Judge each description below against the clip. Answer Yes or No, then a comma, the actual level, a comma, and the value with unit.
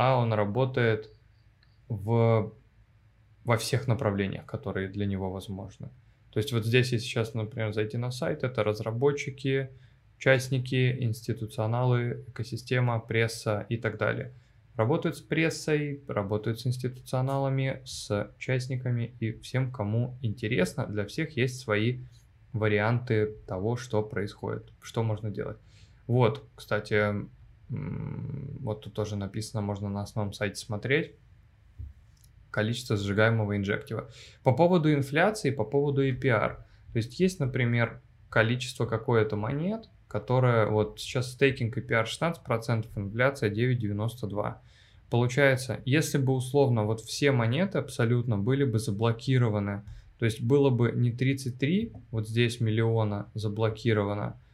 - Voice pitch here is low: Yes, low, 115 Hz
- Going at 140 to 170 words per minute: No, average, 120 wpm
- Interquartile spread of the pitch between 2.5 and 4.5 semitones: Yes, average, 3.2 semitones